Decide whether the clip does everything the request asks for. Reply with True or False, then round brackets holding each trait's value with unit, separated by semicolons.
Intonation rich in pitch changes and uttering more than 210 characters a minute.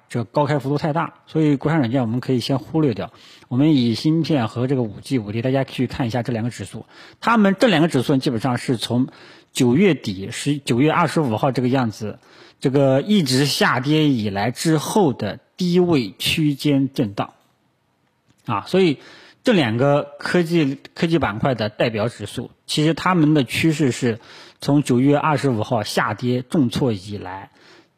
False (4.1 semitones; 265 characters per minute)